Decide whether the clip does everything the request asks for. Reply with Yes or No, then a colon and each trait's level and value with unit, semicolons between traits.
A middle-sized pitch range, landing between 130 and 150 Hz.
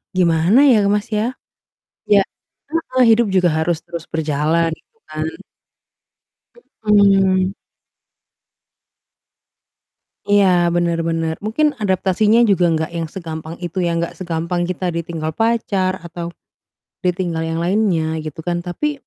No: average, 3.8 semitones; medium, 175 Hz